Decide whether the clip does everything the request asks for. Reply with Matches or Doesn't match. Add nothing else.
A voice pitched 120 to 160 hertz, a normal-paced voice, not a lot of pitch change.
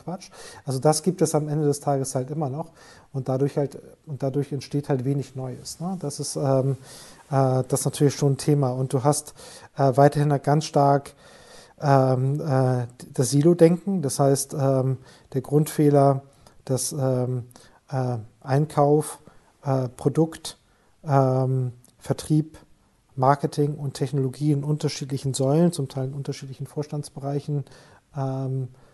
Matches